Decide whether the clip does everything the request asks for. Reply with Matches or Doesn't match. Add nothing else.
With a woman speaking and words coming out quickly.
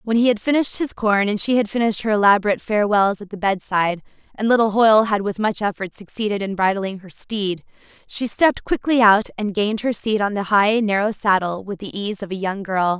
Matches